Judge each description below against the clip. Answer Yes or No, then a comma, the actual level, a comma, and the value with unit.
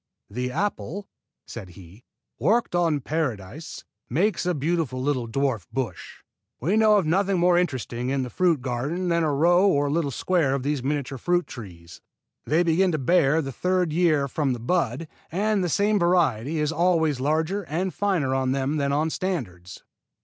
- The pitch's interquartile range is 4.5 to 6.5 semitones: Yes, average, 5.2 semitones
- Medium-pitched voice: Yes, medium, 155 Hz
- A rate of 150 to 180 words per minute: Yes, average, 175 wpm